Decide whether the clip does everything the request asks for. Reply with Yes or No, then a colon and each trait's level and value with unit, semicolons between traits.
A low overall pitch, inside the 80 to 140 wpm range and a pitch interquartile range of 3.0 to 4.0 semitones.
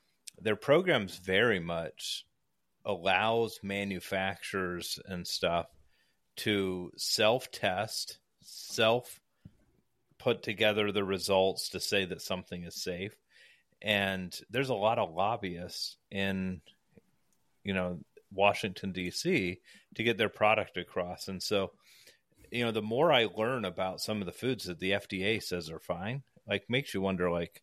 No: very low, 95 Hz; slow, 135 wpm; narrow, 2.5 semitones